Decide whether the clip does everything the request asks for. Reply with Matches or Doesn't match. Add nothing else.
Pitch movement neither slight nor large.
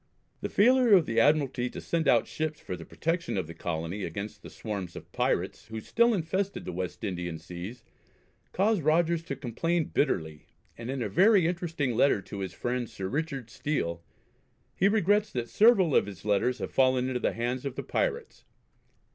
Doesn't match